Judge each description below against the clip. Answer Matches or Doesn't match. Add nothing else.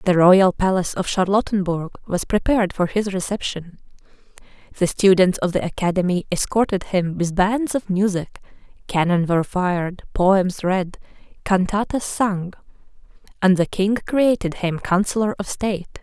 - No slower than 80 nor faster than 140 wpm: Matches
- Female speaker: Matches